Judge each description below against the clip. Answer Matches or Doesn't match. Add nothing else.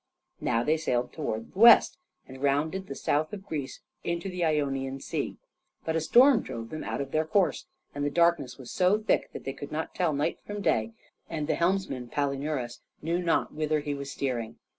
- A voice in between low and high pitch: Matches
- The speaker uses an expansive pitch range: Doesn't match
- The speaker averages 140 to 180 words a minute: Doesn't match